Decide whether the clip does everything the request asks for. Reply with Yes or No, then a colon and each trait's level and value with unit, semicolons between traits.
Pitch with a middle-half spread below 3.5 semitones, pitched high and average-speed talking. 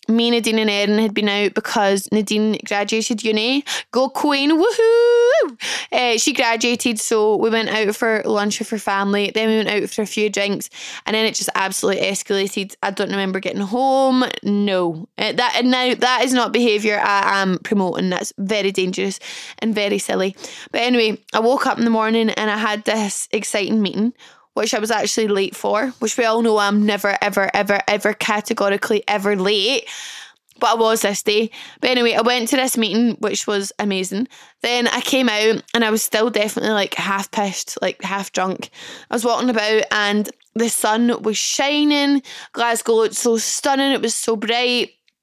Yes: average, 2.7 semitones; high, 220 Hz; average, 190 wpm